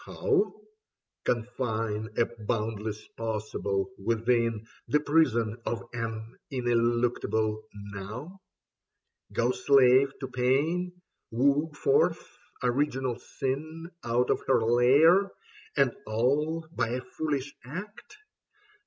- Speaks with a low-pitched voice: Yes, low, 125 Hz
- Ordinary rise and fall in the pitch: Yes, average, 4.5 semitones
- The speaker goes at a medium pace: No, slow, 100 wpm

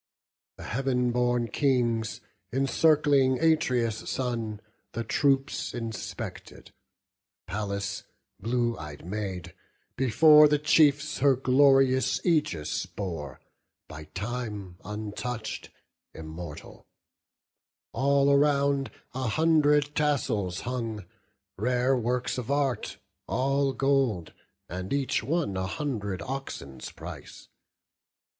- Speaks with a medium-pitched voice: No, low, 125 Hz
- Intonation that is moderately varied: Yes, average, 4.9 semitones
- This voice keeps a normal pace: No, slow, 90 wpm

